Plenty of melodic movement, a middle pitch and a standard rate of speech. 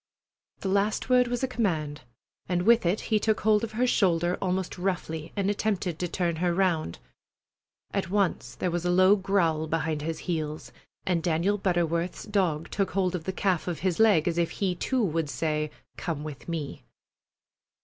No: average, 3.5 semitones; medium, 180 Hz; average, 180 wpm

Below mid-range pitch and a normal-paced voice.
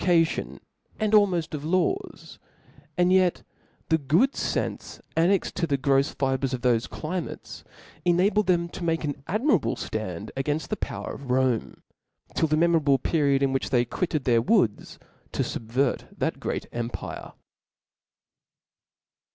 No: medium, 155 Hz; average, 145 wpm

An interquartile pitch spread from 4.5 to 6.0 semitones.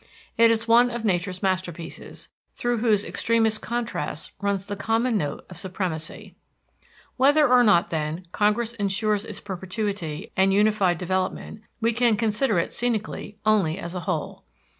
No: average, 3.8 semitones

